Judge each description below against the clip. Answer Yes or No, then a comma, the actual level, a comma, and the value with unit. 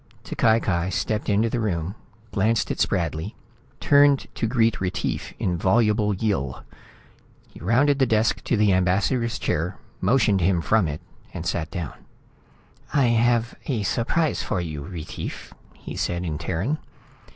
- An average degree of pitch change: Yes, average, 4.9 semitones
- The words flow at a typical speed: Yes, average, 145 wpm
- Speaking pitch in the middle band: No, low, 105 Hz